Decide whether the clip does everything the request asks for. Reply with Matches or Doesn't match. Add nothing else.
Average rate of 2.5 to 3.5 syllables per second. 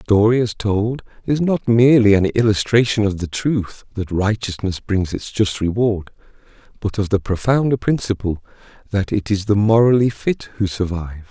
Doesn't match